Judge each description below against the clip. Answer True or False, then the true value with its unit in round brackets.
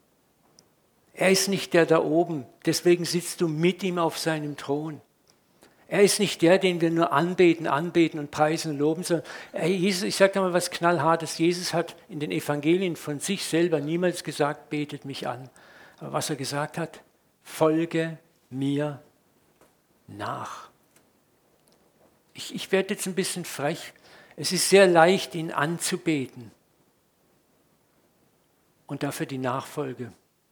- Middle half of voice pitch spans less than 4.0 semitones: True (3.0 semitones)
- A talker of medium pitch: True (165 Hz)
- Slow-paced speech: False (140 wpm)